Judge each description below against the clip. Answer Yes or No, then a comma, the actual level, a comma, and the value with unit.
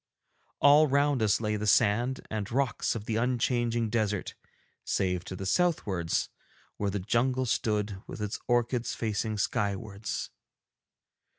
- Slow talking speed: Yes, slow, 130 wpm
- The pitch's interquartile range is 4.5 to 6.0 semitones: No, average, 3.1 semitones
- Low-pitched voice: Yes, low, 110 Hz